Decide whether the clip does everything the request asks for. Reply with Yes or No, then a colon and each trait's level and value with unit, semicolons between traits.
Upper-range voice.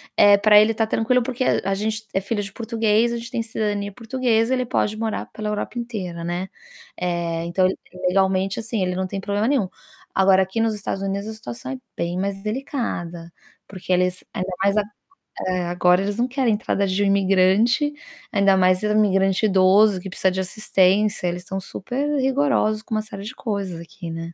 Yes: high, 200 Hz